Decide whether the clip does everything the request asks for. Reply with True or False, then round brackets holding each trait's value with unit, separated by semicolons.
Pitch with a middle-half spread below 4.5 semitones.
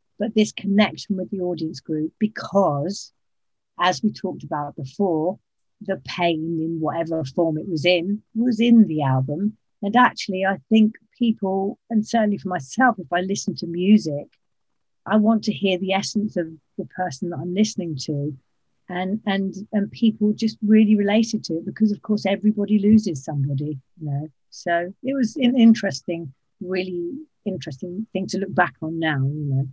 False (4.8 semitones)